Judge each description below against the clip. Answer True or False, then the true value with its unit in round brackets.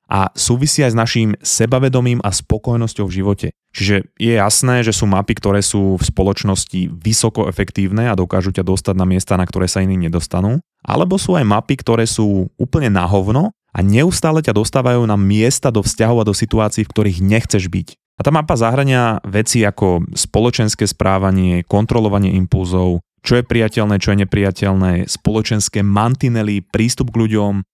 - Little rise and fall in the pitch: False (3.2 semitones)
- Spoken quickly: True (170 wpm)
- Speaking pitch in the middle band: False (105 Hz)